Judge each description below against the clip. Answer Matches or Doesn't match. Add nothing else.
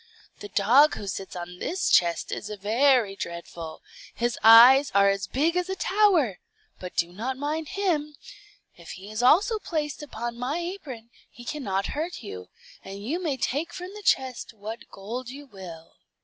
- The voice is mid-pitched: Doesn't match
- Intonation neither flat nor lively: Doesn't match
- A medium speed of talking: Matches